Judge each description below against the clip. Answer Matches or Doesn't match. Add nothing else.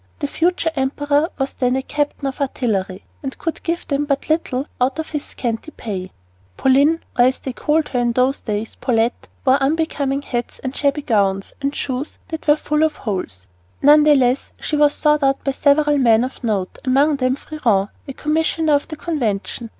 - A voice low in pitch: Doesn't match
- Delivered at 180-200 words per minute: Matches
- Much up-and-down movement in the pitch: Doesn't match